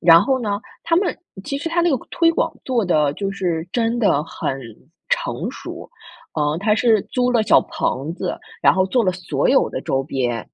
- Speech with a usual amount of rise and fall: No, wide, 7.8 semitones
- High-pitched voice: Yes, high, 205 Hz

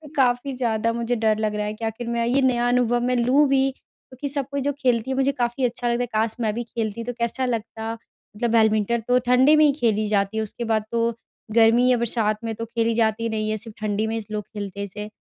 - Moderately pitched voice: No, high, 230 Hz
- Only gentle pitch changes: Yes, narrow, 2.2 semitones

